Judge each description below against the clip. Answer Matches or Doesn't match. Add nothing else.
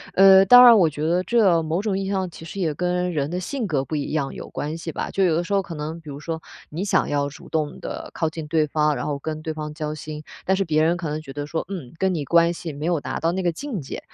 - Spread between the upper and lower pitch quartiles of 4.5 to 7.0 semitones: Doesn't match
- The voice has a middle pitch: Matches